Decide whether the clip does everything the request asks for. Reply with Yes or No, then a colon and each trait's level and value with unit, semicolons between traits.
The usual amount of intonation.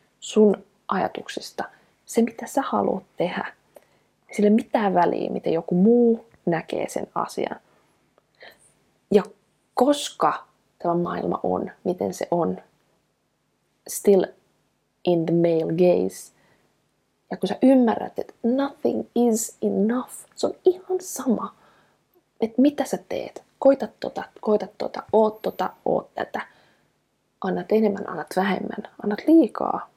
Yes: average, 4.5 semitones